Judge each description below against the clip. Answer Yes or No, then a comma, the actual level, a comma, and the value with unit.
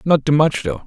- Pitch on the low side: No, medium, 145 Hz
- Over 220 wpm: Yes, fast, 280 wpm